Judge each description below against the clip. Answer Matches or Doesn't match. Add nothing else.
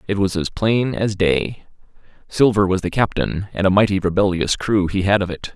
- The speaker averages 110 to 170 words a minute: Doesn't match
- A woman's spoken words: Doesn't match